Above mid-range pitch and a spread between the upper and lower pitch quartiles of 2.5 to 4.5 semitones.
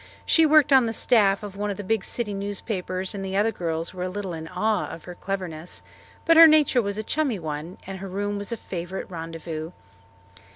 Yes: high, 195 Hz; average, 3.6 semitones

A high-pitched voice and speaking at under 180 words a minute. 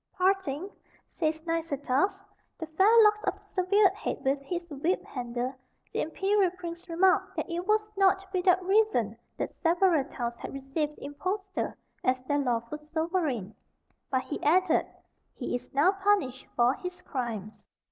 Yes: very high, 330 Hz; average, 150 wpm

